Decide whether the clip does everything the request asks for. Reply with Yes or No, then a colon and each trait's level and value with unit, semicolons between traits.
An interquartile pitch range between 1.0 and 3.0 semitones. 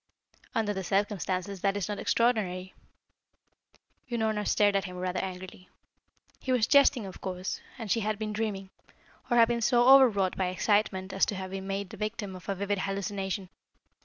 Yes: narrow, 2.5 semitones